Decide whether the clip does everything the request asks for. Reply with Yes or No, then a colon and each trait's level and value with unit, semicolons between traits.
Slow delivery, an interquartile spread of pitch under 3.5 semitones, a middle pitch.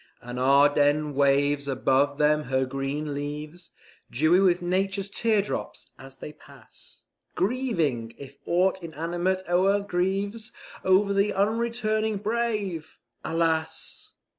No: slow, 110 wpm; wide, 5.6 semitones; medium, 170 Hz